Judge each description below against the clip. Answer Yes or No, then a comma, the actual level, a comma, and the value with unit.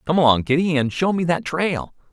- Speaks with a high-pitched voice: No, medium, 155 Hz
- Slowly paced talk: No, fast, 225 wpm